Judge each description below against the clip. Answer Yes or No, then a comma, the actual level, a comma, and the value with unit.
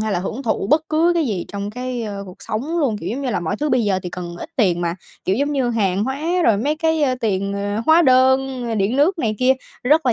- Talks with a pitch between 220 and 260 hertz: Yes, high, 240 Hz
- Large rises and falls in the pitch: Yes, wide, 5.7 semitones